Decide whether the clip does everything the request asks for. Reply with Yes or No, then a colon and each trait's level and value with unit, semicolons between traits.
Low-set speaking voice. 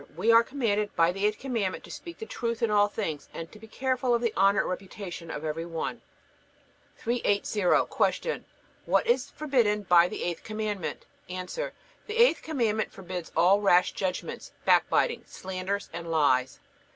No: high, 205 Hz